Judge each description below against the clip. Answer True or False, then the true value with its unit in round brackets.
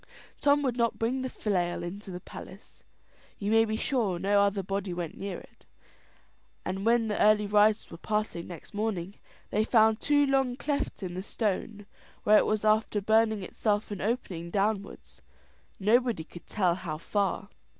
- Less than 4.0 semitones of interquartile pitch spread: True (2.9 semitones)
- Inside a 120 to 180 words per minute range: True (170 wpm)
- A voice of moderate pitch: False (210 Hz)